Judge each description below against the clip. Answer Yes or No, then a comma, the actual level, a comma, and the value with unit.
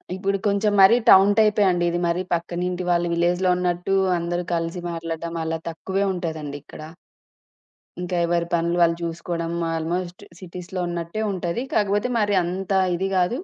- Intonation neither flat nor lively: No, narrow, 2.1 semitones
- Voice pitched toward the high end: No, medium, 175 Hz